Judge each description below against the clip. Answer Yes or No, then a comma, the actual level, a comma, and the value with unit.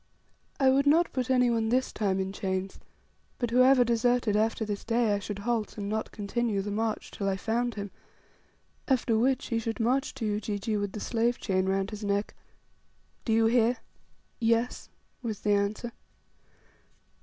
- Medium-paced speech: Yes, average, 170 wpm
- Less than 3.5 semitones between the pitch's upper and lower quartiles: Yes, average, 2.9 semitones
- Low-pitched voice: No, high, 225 Hz